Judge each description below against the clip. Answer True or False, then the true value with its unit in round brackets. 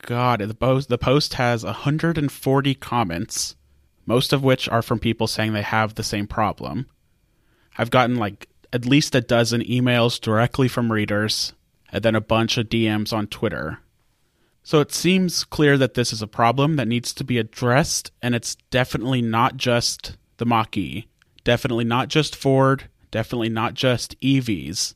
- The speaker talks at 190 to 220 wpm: False (160 wpm)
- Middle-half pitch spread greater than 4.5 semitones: False (2.9 semitones)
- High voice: False (120 Hz)